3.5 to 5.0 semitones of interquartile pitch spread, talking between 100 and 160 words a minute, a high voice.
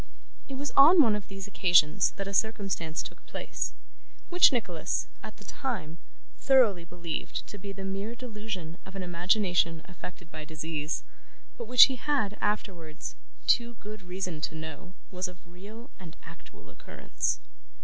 Yes: average, 4.5 semitones; average, 155 wpm; high, 195 Hz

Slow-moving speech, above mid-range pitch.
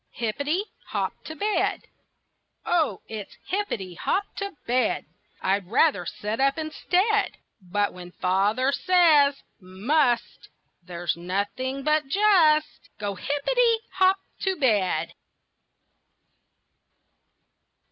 Yes: slow, 95 wpm; very high, 270 Hz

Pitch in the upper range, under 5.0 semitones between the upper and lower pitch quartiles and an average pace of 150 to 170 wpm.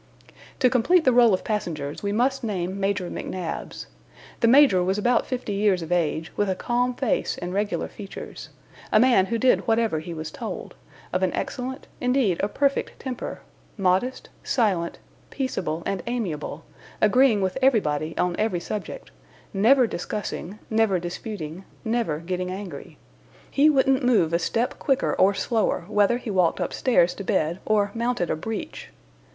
No: high, 205 Hz; average, 5.3 semitones; average, 155 wpm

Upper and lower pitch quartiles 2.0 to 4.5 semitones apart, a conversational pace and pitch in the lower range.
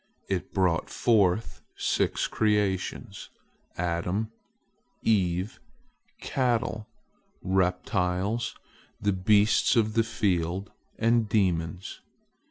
No: average, 3.3 semitones; slow, 75 wpm; low, 100 Hz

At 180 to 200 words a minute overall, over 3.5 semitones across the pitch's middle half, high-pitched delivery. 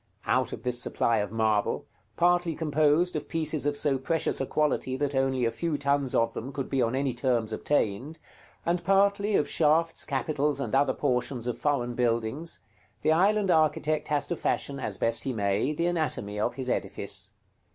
No: average, 185 wpm; average, 4.3 semitones; medium, 140 Hz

